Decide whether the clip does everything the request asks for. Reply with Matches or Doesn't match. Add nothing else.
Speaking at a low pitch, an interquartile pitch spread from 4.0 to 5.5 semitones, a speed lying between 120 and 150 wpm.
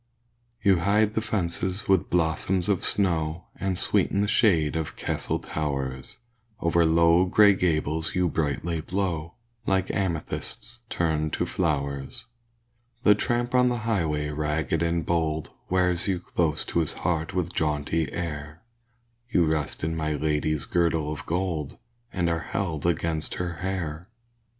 Doesn't match